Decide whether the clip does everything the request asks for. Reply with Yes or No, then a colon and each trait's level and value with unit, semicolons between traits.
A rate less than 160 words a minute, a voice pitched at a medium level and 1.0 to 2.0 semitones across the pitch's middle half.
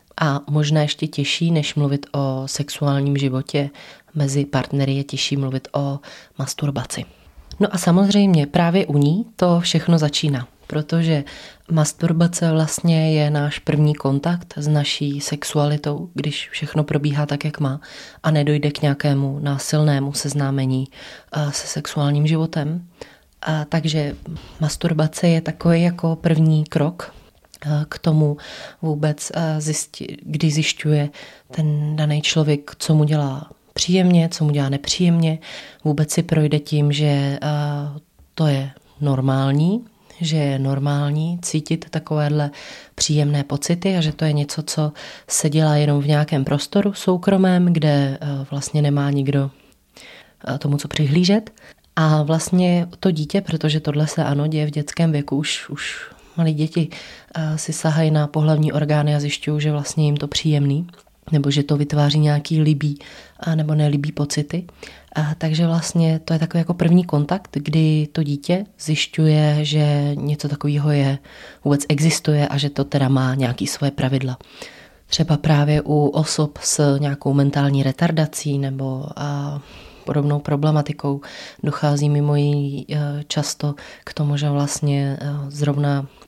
Yes: average, 135 wpm; medium, 150 Hz; narrow, 1.7 semitones